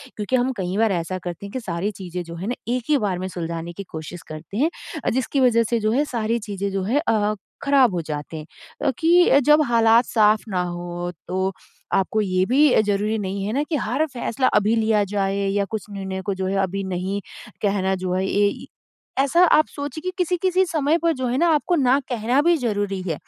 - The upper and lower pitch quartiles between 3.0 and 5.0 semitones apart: No, wide, 5.4 semitones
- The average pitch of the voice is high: Yes, high, 210 Hz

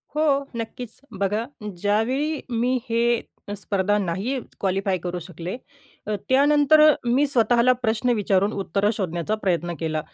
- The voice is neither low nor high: No, high, 215 Hz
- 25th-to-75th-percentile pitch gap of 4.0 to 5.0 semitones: Yes, average, 4.7 semitones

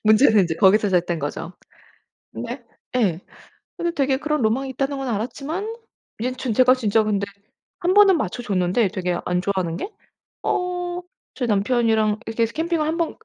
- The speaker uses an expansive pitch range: Yes, wide, 6.3 semitones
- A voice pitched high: Yes, high, 230 Hz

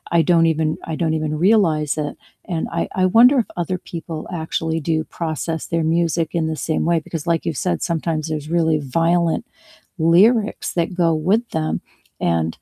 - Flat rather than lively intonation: Yes, narrow, 1.5 semitones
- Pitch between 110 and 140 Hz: No, medium, 165 Hz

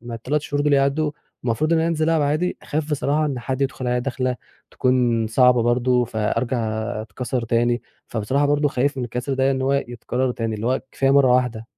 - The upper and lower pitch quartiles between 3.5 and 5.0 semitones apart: No, average, 2.9 semitones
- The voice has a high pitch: No, low, 130 Hz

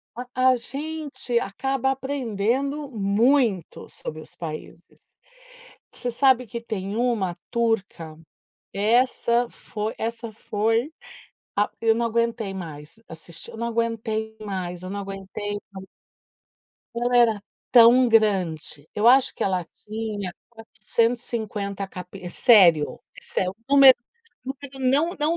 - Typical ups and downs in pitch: Yes, average, 3.7 semitones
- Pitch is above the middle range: Yes, high, 225 Hz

